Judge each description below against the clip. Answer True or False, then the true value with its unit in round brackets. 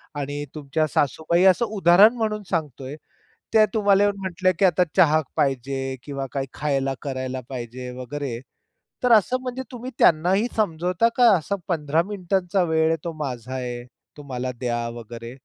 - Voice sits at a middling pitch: True (155 Hz)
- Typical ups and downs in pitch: False (6.3 semitones)